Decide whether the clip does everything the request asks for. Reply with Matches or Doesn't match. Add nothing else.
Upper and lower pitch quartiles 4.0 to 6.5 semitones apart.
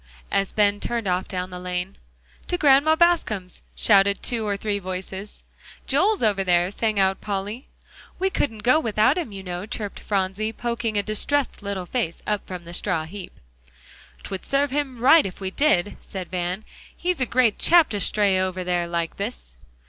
Matches